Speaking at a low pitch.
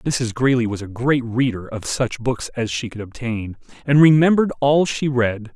Yes: low, 125 Hz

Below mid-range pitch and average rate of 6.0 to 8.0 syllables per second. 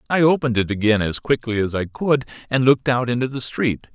Yes: low, 120 Hz; 6.1 syllables/s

